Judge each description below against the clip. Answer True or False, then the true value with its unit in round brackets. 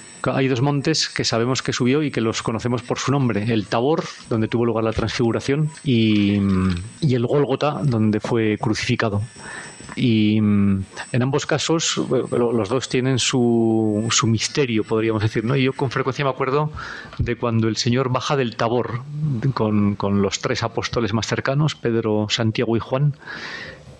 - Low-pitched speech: True (120 Hz)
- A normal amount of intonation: True (3.3 semitones)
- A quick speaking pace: False (165 wpm)